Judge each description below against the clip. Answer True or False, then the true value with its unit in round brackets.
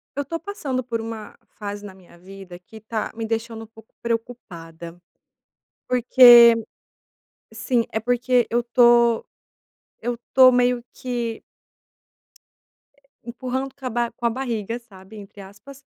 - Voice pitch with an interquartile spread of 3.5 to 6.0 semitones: False (2.5 semitones)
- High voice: True (235 Hz)